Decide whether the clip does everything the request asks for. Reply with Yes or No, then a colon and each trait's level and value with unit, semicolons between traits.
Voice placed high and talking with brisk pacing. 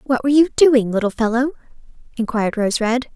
No: high, 245 Hz; average, 170 wpm